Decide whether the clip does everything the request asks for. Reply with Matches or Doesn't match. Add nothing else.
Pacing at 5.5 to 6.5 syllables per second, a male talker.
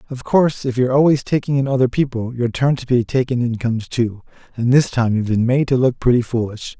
Matches